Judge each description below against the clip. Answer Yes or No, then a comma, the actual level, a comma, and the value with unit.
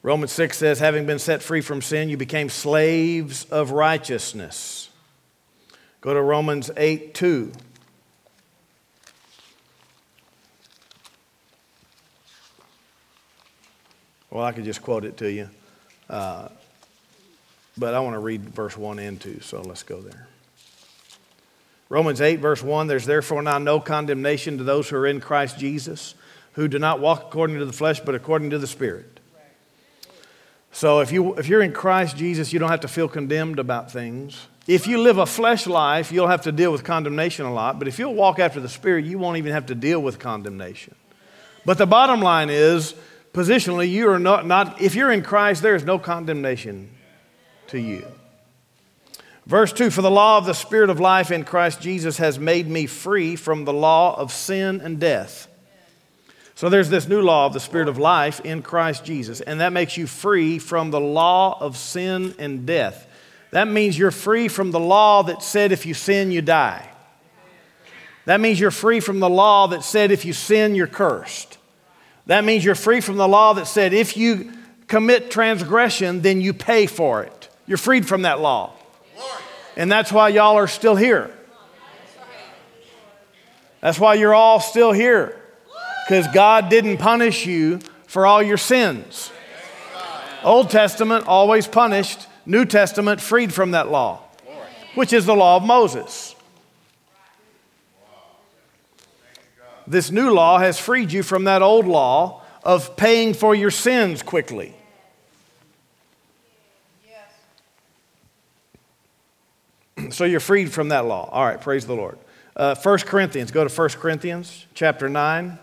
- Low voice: No, medium, 175 Hz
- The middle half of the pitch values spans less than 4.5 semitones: No, wide, 5.4 semitones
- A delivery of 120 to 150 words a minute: No, average, 160 wpm